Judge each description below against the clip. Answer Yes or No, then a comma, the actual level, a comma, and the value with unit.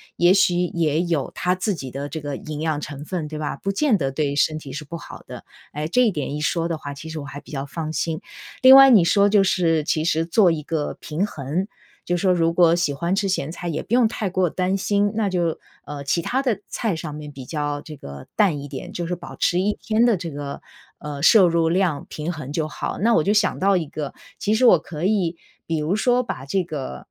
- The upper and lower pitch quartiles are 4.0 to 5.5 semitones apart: Yes, average, 4.4 semitones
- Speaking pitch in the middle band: Yes, medium, 165 Hz